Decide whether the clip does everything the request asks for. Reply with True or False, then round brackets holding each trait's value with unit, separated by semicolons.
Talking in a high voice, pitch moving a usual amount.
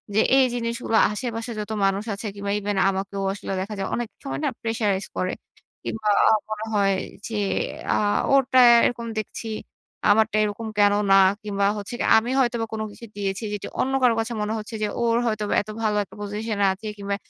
False (215 Hz; 2.3 semitones)